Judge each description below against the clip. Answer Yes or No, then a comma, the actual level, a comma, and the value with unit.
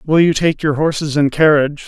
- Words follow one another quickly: Yes, fast, 225 wpm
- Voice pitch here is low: No, medium, 150 Hz